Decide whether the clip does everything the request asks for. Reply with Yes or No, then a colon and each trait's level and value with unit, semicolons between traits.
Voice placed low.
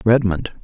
Yes: low, 105 Hz